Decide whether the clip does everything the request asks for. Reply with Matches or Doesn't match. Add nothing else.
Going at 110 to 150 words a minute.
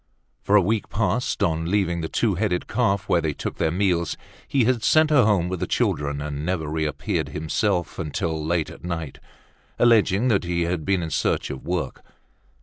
Doesn't match